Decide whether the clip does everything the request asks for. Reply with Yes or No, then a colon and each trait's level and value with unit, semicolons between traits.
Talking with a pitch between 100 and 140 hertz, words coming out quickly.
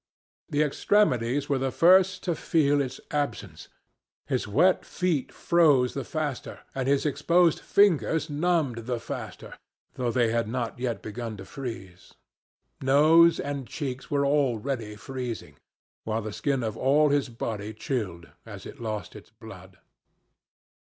No: low, 135 Hz; average, 140 wpm